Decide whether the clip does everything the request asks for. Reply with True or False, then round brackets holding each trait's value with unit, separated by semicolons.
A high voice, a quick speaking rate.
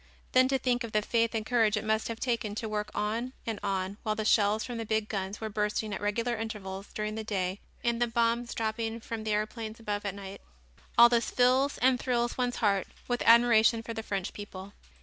True (220 Hz; 220 wpm)